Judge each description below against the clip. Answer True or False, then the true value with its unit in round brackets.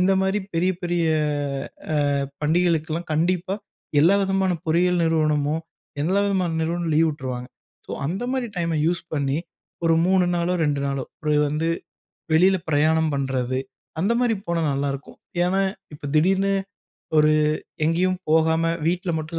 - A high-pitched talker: False (165 Hz)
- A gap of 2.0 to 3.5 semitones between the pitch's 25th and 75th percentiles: True (3.1 semitones)